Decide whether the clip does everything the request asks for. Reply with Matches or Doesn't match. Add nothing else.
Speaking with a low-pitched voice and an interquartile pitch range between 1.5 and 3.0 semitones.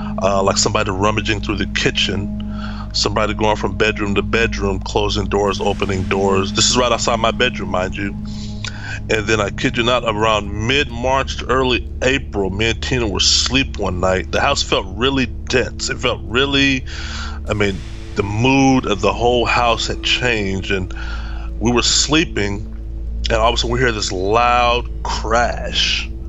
Matches